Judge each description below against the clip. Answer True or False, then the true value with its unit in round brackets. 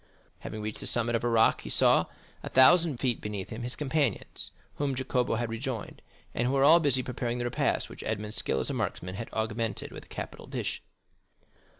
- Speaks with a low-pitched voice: True (120 Hz)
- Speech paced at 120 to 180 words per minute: False (205 wpm)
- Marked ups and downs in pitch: False (3.0 semitones)